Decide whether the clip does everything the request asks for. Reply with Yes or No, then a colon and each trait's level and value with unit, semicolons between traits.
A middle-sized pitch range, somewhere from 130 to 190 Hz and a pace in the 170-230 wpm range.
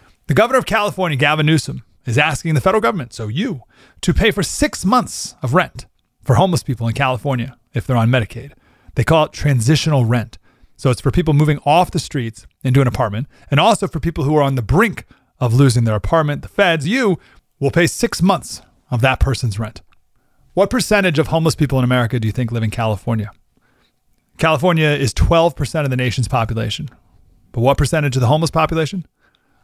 Yes: average, 4.9 semitones; medium, 140 Hz; average, 195 wpm